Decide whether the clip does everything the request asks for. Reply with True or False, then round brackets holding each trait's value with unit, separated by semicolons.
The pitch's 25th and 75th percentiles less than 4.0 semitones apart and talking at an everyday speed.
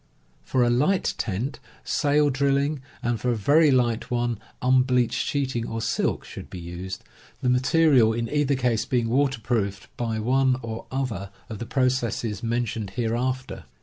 True (2.8 semitones; 155 wpm)